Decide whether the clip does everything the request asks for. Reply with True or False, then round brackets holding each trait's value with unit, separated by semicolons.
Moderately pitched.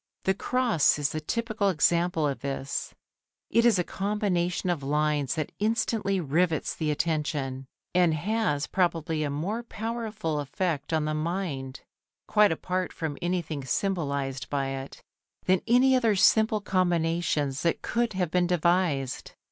True (170 Hz)